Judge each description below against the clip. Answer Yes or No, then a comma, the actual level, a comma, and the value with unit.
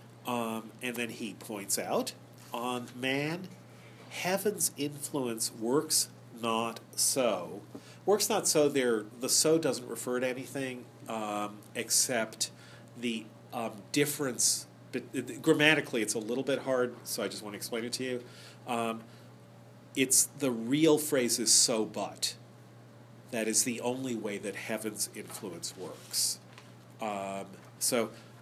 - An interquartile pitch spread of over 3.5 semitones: No, average, 3.1 semitones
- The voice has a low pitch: Yes, low, 120 Hz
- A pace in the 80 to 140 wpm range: Yes, slow, 135 wpm